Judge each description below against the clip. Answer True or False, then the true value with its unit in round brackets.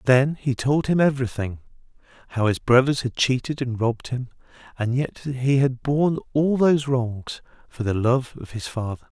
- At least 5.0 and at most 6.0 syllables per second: True (5.1 syllables/s)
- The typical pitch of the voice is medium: False (125 Hz)